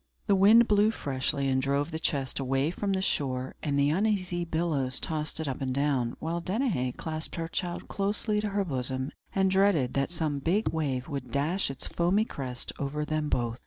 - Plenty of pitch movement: Yes, wide, 5.7 semitones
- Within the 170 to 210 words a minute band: Yes, average, 195 wpm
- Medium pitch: Yes, medium, 155 Hz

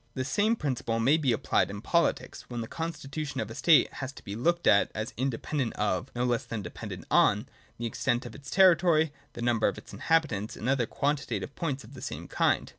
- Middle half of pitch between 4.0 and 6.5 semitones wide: Yes, average, 5.2 semitones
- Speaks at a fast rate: Yes, fast, 215 wpm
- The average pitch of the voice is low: Yes, low, 130 Hz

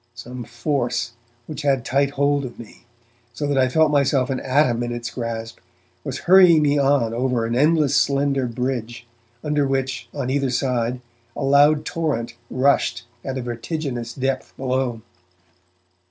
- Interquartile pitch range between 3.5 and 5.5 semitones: No, average, 3.0 semitones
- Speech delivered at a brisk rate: No, average, 155 wpm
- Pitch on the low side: Yes, low, 130 Hz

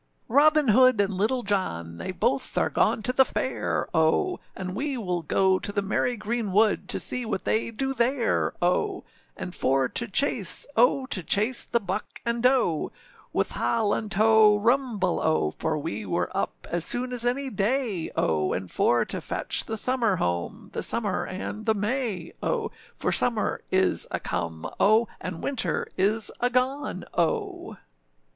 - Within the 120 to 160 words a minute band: No, average, 175 wpm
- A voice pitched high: Yes, high, 220 Hz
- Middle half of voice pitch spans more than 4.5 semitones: Yes, average, 5.2 semitones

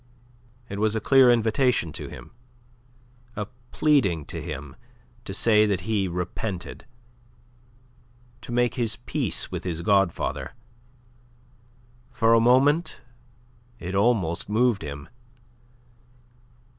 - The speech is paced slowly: Yes, slow, 105 wpm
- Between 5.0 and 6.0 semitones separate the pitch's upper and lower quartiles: Yes, wide, 5.5 semitones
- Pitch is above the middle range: No, low, 105 Hz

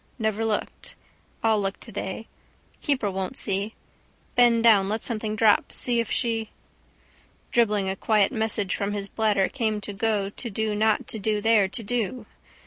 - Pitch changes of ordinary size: No, narrow, 1.9 semitones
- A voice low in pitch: No, high, 215 Hz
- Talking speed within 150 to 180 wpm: Yes, average, 160 wpm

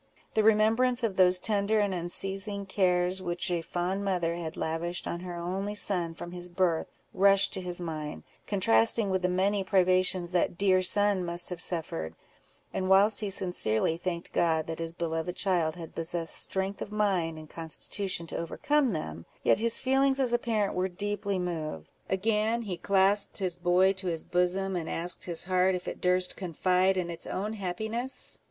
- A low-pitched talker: No, medium, 185 Hz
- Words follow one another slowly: No, average, 180 wpm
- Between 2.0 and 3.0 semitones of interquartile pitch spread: Yes, narrow, 2.6 semitones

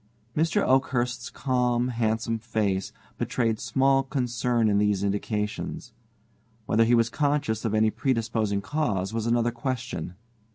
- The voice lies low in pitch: Yes, low, 115 Hz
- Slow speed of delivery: Yes, slow, 125 wpm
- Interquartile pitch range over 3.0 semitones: No, average, 2.7 semitones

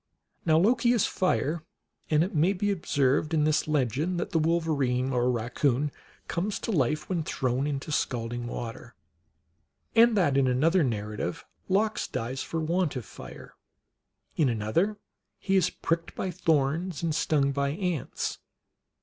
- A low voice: No, medium, 155 Hz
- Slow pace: No, average, 150 wpm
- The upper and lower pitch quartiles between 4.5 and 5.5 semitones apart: Yes, average, 5.2 semitones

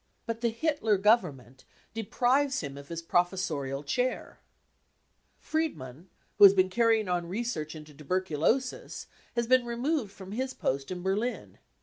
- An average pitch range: No, wide, 7.3 semitones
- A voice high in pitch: Yes, high, 195 Hz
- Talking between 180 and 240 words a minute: No, slow, 135 wpm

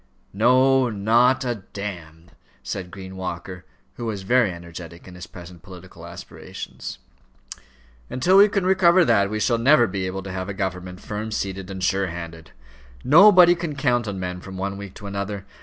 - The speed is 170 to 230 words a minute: Yes, average, 180 wpm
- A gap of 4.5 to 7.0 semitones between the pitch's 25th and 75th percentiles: Yes, average, 5.2 semitones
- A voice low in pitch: Yes, low, 100 Hz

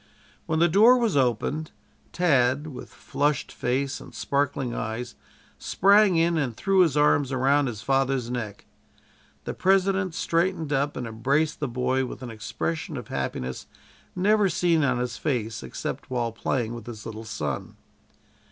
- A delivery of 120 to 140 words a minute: No, average, 150 wpm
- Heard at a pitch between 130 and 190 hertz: Yes, low, 135 Hz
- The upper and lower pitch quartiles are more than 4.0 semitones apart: Yes, wide, 5.5 semitones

